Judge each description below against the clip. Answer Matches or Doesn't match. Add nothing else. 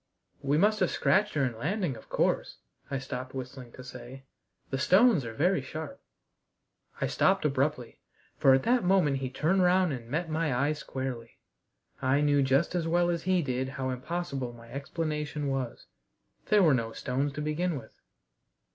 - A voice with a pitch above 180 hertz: Doesn't match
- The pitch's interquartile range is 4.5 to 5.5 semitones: Matches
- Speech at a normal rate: Matches